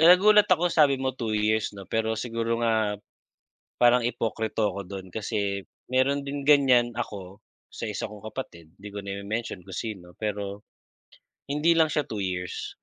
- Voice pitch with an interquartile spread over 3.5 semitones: Yes, average, 4.7 semitones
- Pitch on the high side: No, low, 110 Hz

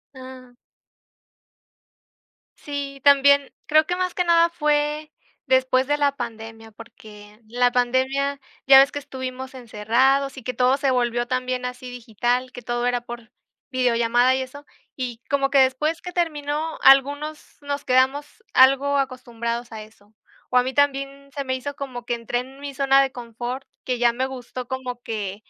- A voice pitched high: Yes, very high, 260 Hz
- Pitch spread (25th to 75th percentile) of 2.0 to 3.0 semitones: Yes, narrow, 2.5 semitones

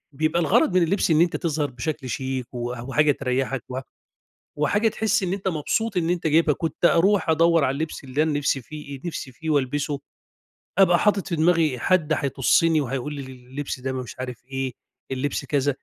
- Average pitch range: Yes, average, 3.9 semitones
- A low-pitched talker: No, medium, 150 Hz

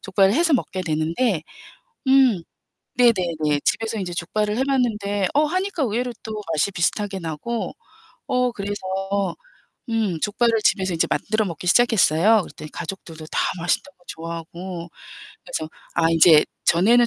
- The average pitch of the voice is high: Yes, high, 200 Hz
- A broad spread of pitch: Yes, wide, 5.7 semitones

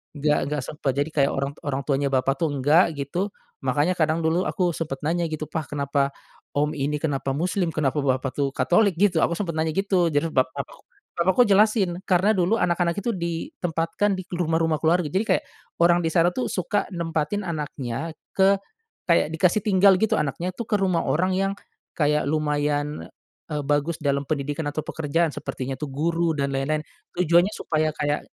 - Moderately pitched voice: Yes, medium, 160 Hz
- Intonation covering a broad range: No, average, 3.5 semitones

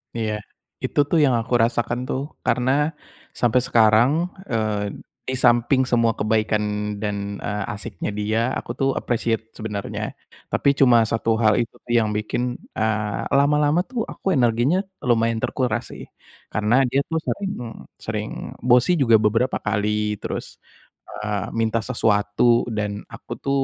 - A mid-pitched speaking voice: No, low, 115 Hz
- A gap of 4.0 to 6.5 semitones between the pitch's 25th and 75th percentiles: No, average, 2.7 semitones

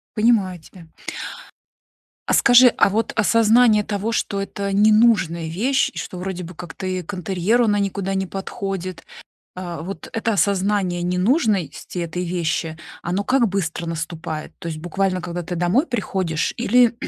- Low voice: No, high, 190 Hz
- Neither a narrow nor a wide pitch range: Yes, average, 3.5 semitones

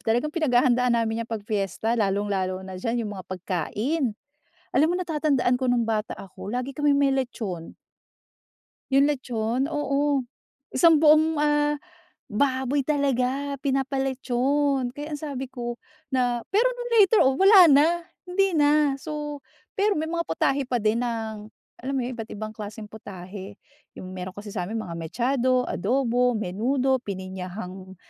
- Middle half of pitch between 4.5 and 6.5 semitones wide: Yes, average, 5.0 semitones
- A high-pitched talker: Yes, very high, 250 Hz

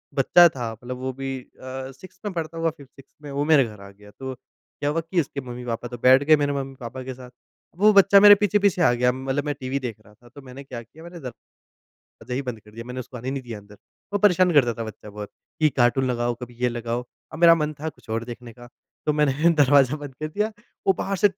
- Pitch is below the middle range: Yes, low, 130 Hz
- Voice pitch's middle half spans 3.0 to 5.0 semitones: Yes, average, 4.1 semitones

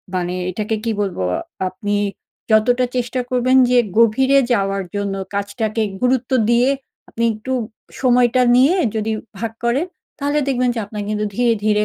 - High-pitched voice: Yes, high, 230 Hz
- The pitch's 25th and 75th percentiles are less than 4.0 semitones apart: Yes, average, 3.3 semitones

